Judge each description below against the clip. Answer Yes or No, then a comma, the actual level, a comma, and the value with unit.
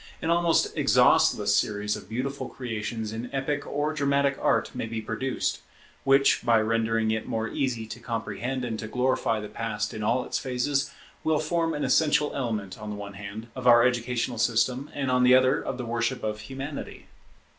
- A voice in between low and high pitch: No, low, 120 Hz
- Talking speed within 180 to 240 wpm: Yes, average, 185 wpm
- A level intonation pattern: No, average, 3.5 semitones